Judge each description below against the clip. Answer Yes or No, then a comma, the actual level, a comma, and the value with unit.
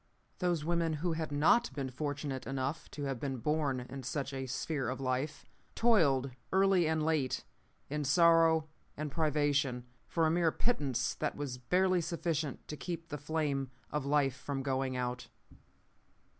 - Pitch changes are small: No, average, 3.2 semitones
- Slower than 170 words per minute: Yes, average, 155 wpm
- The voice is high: No, medium, 145 Hz